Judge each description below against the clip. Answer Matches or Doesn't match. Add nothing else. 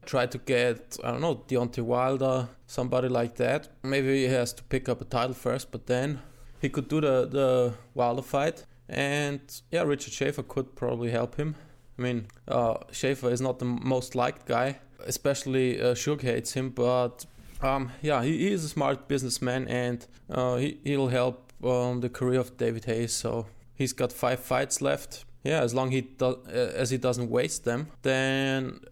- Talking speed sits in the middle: Matches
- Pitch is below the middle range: Matches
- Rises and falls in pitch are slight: Matches